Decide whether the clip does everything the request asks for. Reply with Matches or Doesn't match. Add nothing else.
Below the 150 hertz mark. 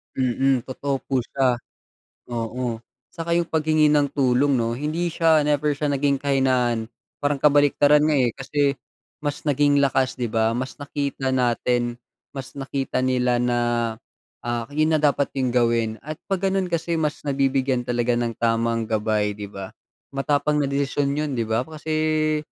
Matches